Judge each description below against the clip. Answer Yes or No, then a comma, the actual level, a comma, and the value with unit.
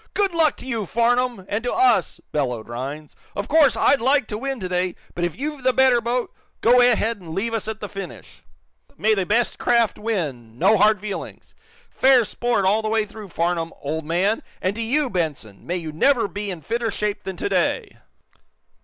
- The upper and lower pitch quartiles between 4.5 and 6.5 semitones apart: Yes, wide, 5.4 semitones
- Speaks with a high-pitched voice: Yes, high, 215 Hz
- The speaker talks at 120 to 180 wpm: No, average, 195 wpm